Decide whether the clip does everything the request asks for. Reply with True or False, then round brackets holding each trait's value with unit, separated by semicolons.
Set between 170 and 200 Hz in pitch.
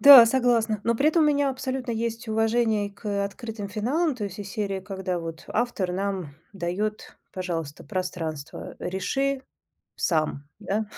False (210 Hz)